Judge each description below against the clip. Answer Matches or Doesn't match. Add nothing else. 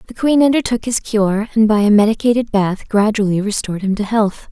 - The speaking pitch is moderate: Doesn't match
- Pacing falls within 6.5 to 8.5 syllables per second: Doesn't match